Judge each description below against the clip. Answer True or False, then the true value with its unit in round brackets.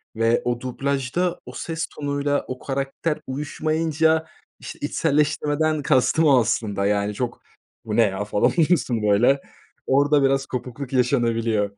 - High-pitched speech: False (135 Hz)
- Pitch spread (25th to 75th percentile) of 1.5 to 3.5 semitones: False (4.3 semitones)